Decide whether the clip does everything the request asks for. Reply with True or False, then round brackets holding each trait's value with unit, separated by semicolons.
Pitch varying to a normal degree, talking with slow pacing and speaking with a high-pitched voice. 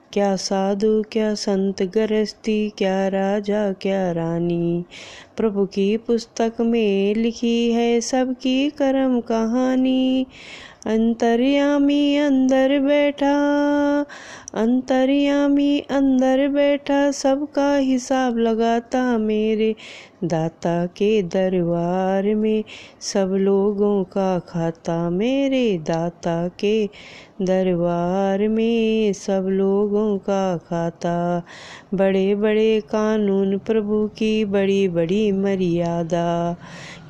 True (4.7 semitones; 80 wpm; 215 Hz)